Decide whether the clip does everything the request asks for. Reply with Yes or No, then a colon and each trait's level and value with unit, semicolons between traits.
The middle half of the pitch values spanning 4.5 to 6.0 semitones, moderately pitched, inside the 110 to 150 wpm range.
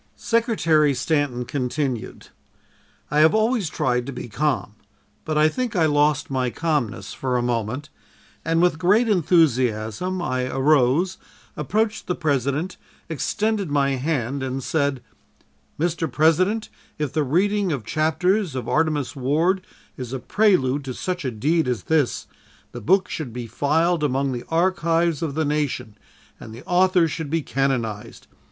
Yes: average, 5.0 semitones; medium, 150 Hz; average, 145 wpm